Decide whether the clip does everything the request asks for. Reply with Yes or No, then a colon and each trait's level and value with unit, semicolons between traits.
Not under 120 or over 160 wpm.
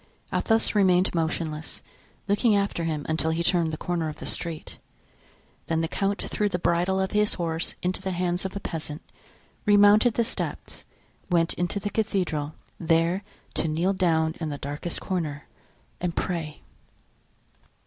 Yes: average, 155 wpm